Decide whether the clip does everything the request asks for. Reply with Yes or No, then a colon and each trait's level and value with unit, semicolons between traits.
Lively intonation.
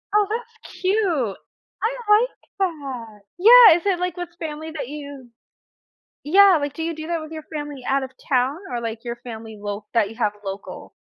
Yes: wide, 7.1 semitones